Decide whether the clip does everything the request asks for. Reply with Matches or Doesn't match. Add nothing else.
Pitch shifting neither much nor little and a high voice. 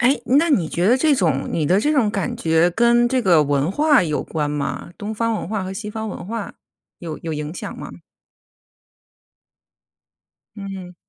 Doesn't match